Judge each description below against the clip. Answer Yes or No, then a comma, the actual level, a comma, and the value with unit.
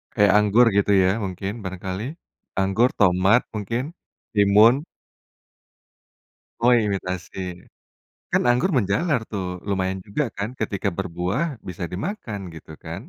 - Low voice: Yes, low, 100 Hz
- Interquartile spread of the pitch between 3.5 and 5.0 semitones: Yes, average, 3.8 semitones